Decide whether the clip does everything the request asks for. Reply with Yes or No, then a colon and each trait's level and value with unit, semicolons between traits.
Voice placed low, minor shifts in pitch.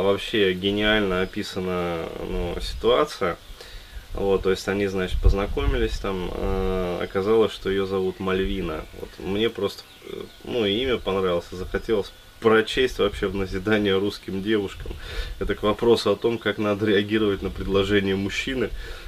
Yes: very low, 95 Hz; narrow, 1.7 semitones